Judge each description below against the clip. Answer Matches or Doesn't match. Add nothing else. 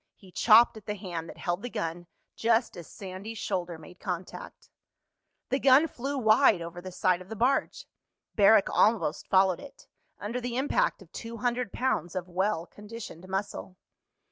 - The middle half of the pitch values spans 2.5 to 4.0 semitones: Doesn't match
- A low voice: Doesn't match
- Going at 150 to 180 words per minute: Matches